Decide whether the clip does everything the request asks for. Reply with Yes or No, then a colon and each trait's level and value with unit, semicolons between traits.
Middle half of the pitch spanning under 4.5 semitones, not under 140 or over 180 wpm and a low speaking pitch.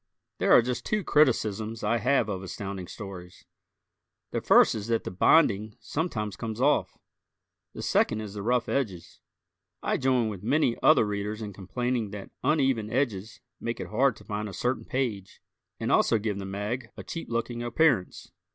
Yes: average, 3.6 semitones; average, 170 wpm; low, 110 Hz